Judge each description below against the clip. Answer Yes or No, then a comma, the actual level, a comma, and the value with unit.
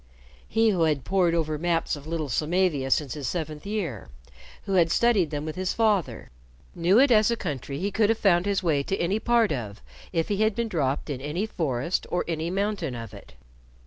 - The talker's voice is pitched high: No, medium, 170 Hz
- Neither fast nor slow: No, fast, 210 wpm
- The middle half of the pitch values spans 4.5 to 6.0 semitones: Yes, average, 5.2 semitones